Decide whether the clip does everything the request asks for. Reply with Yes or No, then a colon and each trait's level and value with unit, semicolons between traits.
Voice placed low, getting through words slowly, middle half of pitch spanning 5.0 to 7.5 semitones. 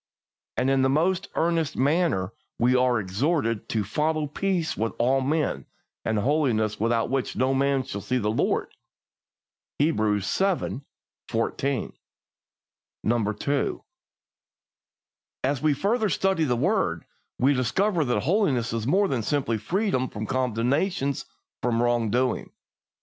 Yes: low, 130 Hz; slow, 130 wpm; average, 5.3 semitones